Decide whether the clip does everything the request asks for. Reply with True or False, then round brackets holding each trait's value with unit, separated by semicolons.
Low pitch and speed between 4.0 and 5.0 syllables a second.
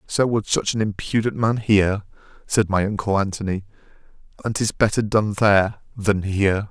False (100 Hz; 5.2 syllables/s)